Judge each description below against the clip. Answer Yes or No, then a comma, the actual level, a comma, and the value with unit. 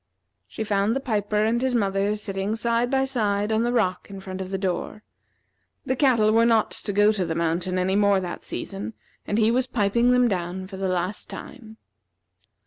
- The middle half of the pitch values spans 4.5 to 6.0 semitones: No, average, 3.3 semitones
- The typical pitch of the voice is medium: No, high, 210 Hz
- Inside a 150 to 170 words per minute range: No, average, 200 wpm